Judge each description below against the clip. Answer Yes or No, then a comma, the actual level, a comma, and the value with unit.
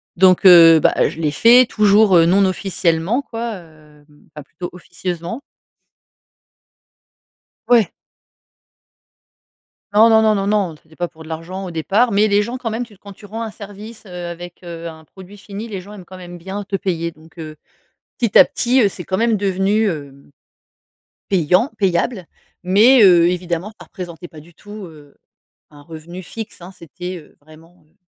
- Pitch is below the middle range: No, medium, 185 Hz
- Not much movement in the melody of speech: No, average, 3.8 semitones